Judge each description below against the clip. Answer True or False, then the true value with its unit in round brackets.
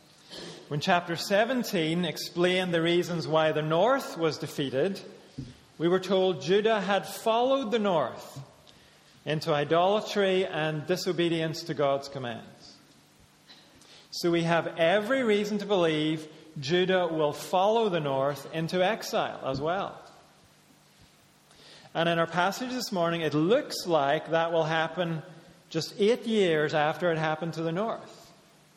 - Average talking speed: False (130 wpm)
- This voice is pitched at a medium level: True (170 Hz)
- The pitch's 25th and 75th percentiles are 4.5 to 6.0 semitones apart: False (3.3 semitones)